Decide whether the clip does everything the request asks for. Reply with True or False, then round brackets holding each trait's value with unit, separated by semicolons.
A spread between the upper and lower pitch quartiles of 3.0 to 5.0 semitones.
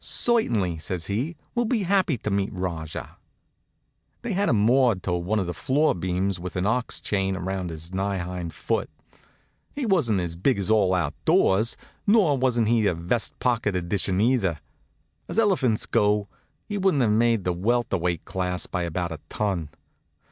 False (5.6 semitones)